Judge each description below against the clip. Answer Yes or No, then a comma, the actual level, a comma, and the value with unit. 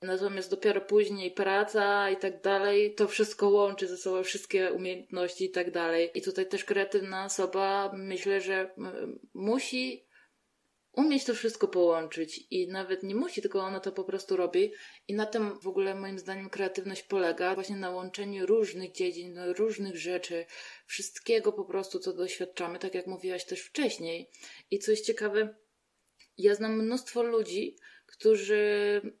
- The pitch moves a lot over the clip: No, average, 2.8 semitones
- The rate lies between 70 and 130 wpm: No, average, 150 wpm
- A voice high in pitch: Yes, high, 195 Hz